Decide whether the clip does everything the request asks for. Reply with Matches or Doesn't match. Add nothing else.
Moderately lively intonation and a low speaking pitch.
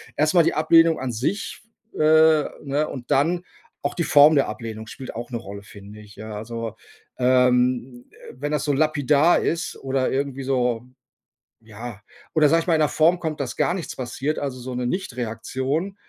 Matches